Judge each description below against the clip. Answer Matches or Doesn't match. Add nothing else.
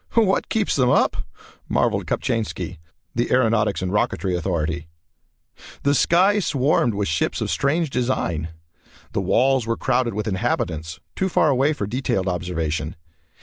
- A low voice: Matches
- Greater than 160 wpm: Doesn't match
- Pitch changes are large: Matches